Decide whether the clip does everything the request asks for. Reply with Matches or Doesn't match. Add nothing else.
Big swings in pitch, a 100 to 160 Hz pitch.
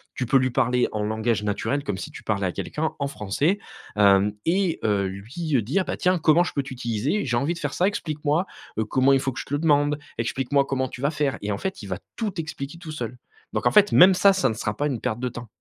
Matches